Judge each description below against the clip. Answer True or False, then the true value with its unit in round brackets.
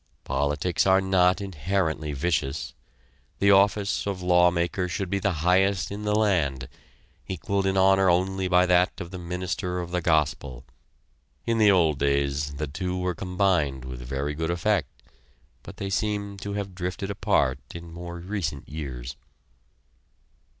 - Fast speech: False (150 wpm)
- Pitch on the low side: True (90 Hz)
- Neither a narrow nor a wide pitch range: True (4.2 semitones)